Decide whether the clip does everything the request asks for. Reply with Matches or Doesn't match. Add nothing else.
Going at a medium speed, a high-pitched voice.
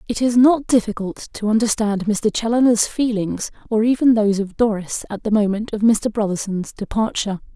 Matches